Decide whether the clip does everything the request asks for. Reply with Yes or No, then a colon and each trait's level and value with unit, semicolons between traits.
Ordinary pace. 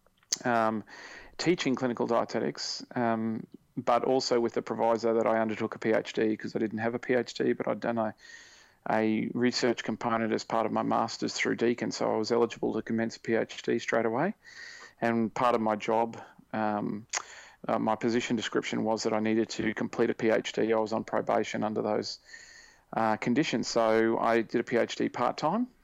Yes: average, 180 wpm